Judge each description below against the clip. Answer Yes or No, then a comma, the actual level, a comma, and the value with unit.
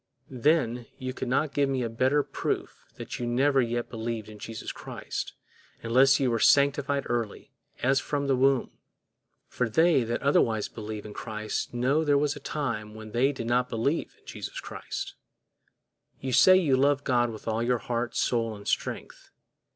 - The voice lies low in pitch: Yes, low, 125 Hz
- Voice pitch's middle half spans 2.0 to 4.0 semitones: Yes, average, 3.4 semitones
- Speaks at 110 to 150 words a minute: No, average, 175 wpm